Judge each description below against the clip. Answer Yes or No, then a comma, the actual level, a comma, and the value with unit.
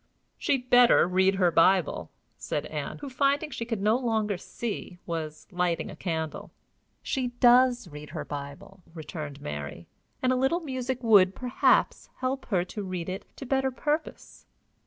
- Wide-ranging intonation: Yes, wide, 6.7 semitones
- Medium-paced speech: Yes, average, 155 wpm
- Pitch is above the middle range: Yes, high, 210 Hz